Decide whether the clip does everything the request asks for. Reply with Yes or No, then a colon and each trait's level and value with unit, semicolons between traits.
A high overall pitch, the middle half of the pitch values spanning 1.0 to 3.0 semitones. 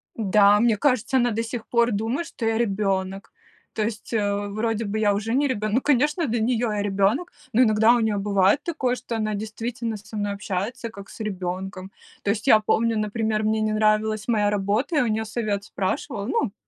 Yes: high, 215 Hz; narrow, 2.4 semitones